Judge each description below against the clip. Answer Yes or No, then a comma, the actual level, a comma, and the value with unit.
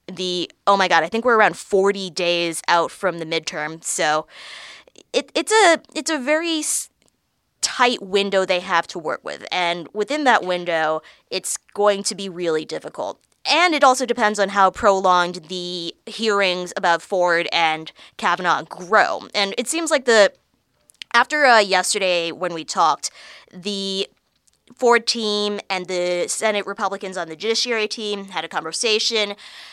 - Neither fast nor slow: Yes, average, 155 wpm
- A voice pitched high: Yes, high, 195 Hz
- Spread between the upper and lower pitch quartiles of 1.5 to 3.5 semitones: No, average, 4.3 semitones